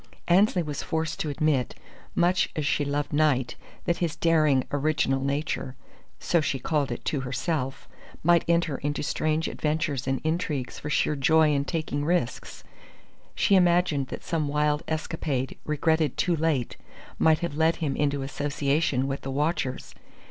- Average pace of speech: Yes, average, 155 wpm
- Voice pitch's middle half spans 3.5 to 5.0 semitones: No, narrow, 2.5 semitones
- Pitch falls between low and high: Yes, medium, 150 Hz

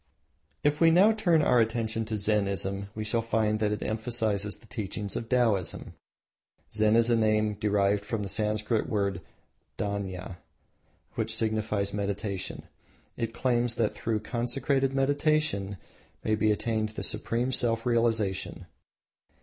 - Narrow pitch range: Yes, narrow, 2.3 semitones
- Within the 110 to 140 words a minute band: Yes, slow, 135 wpm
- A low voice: Yes, low, 110 Hz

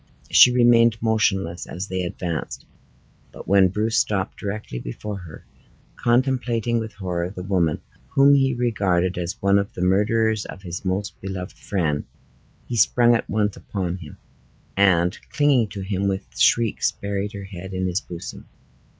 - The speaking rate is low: No, average, 155 wpm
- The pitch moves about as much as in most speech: Yes, average, 3.5 semitones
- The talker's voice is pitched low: Yes, low, 100 Hz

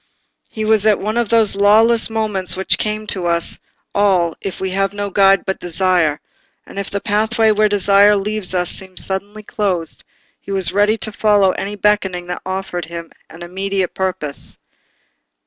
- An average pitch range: No, narrow, 2.3 semitones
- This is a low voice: No, high, 195 Hz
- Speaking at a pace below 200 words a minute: Yes, average, 170 wpm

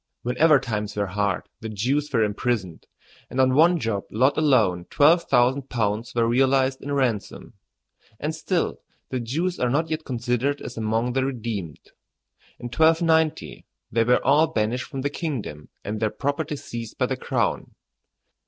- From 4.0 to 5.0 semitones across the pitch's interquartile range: Yes, average, 4.3 semitones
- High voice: No, low, 125 Hz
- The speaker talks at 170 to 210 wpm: No, average, 160 wpm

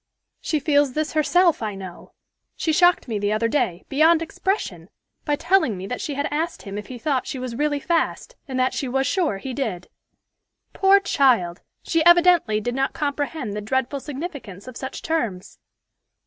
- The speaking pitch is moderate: No, very high, 275 Hz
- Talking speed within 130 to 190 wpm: Yes, average, 180 wpm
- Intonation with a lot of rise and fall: Yes, wide, 6.0 semitones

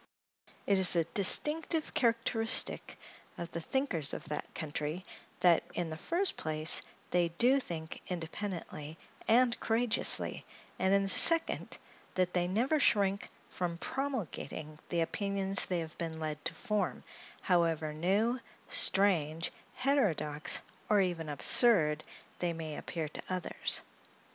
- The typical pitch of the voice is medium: Yes, medium, 180 Hz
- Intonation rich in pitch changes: Yes, wide, 5.7 semitones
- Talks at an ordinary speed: No, slow, 130 wpm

